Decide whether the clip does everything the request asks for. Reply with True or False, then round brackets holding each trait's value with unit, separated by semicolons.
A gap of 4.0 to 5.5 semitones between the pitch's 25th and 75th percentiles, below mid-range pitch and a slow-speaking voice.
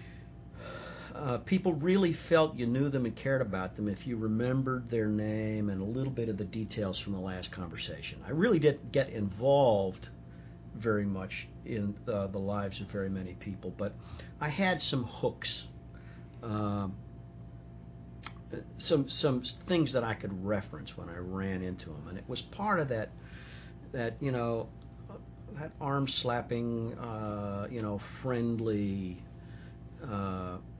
False (5.1 semitones; 105 Hz; 150 wpm)